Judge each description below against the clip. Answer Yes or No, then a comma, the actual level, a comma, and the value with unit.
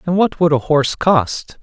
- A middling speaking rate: No, fast, 220 wpm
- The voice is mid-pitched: Yes, medium, 155 Hz